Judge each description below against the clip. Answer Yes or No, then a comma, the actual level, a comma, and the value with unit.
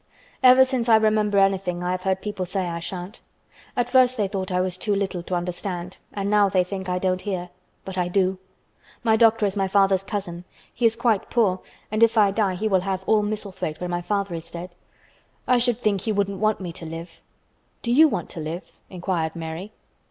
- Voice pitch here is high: Yes, high, 195 Hz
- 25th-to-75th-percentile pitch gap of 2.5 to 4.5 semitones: Yes, average, 2.9 semitones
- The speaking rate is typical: No, fast, 215 wpm